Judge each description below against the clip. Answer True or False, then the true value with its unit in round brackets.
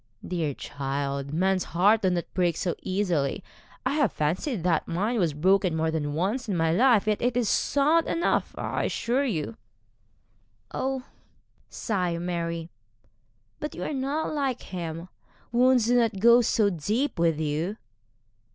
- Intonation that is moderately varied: False (6.6 semitones)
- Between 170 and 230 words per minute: False (150 wpm)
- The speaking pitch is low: False (185 Hz)